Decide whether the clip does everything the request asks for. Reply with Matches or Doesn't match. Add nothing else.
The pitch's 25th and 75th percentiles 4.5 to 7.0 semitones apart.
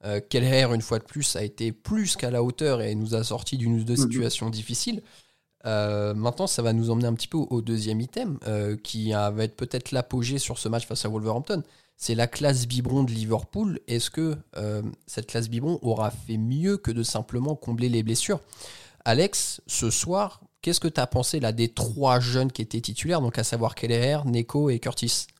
Doesn't match